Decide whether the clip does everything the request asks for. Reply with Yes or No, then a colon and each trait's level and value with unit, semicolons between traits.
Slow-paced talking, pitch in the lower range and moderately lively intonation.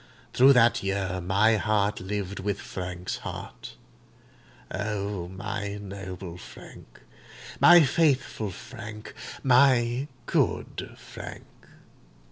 Yes: slow, 85 wpm; low, 105 Hz; average, 3.7 semitones